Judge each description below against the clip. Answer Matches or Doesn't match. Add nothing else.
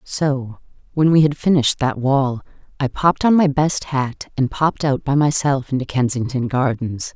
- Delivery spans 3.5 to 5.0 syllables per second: Matches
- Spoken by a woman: Matches